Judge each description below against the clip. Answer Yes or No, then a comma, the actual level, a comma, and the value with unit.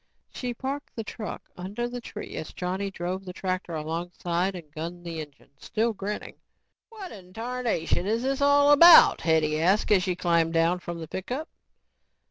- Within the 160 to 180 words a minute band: Yes, average, 170 wpm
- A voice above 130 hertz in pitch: Yes, medium, 185 Hz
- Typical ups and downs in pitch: No, wide, 5.7 semitones